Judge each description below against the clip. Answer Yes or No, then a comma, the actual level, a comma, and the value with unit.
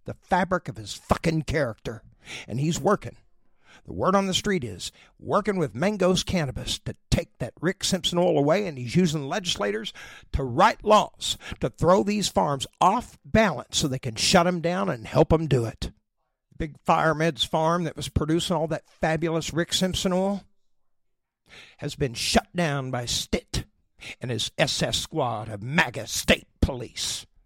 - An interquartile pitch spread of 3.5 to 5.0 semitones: Yes, average, 4.6 semitones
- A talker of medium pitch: Yes, medium, 160 Hz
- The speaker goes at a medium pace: Yes, average, 170 wpm